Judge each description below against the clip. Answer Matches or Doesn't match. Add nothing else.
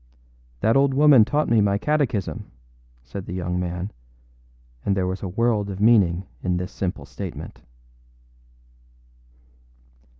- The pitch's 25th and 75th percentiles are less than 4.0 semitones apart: Doesn't match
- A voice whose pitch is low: Matches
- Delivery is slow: Matches